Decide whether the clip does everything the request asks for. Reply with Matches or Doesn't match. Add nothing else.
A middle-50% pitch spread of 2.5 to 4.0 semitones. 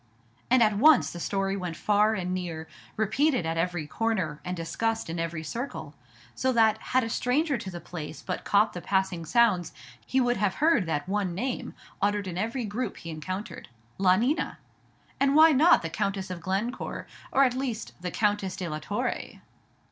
Doesn't match